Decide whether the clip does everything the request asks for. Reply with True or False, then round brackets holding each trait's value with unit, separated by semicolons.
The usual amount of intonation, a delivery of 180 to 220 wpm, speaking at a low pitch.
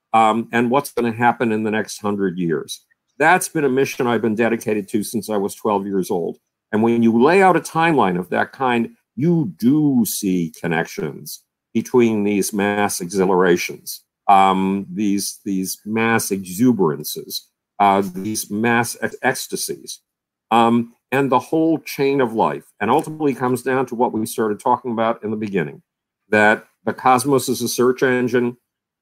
False (3.5 semitones; 165 wpm; 115 Hz)